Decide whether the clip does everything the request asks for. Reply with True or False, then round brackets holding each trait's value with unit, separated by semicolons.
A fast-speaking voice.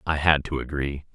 True (210 wpm)